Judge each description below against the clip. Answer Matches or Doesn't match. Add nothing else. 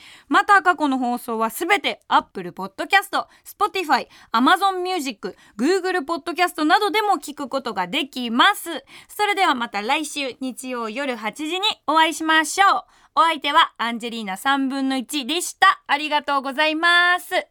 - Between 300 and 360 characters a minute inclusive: Doesn't match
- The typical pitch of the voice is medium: Doesn't match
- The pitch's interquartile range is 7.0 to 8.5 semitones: Doesn't match